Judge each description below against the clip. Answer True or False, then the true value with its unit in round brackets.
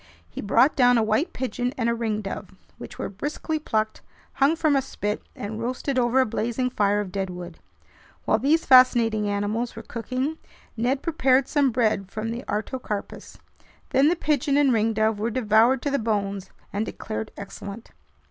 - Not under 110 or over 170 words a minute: True (165 wpm)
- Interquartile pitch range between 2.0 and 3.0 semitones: False (3.7 semitones)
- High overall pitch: True (230 Hz)